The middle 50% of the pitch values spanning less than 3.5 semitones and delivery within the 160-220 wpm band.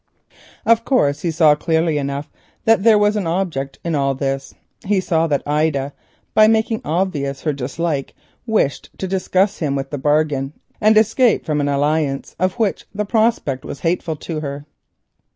No: wide, 5.5 semitones; average, 165 wpm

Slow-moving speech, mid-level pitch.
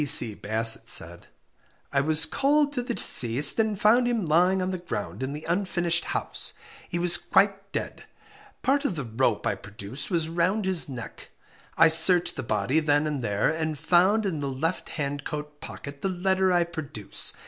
No: average, 180 wpm; medium, 165 Hz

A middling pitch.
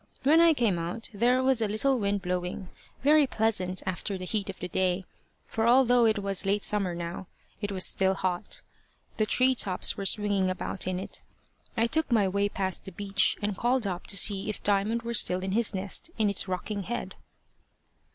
No: high, 200 Hz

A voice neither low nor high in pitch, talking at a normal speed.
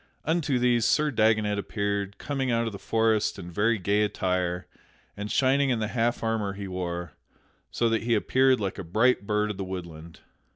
No: low, 105 Hz; average, 190 wpm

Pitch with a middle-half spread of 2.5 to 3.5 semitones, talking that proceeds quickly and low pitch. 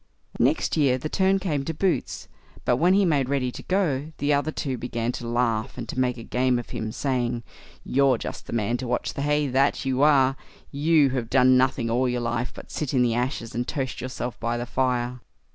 Yes: average, 2.8 semitones; fast, 220 wpm; low, 130 Hz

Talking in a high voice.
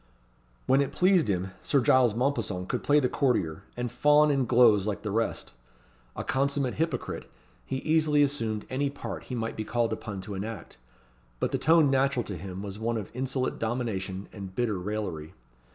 No: low, 120 Hz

